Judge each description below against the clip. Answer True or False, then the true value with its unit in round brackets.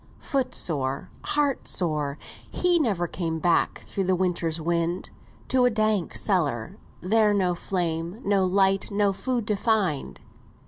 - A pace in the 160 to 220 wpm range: False (140 wpm)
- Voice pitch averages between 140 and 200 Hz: True (185 Hz)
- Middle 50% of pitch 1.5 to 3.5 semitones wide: False (4.4 semitones)